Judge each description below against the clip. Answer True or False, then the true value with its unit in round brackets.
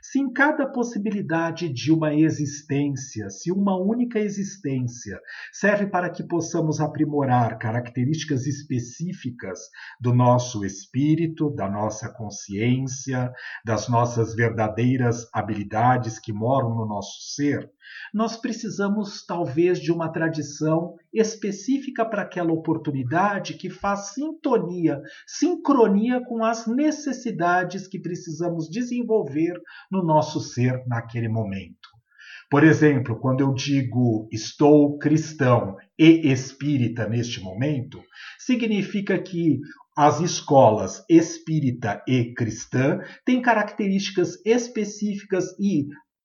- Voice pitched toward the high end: False (155 Hz)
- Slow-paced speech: True (105 wpm)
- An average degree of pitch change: False (7.9 semitones)